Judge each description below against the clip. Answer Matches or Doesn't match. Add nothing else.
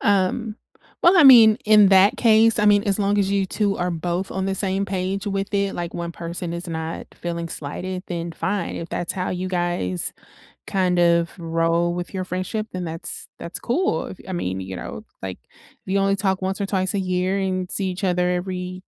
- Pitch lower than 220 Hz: Matches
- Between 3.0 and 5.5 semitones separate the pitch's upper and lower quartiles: Doesn't match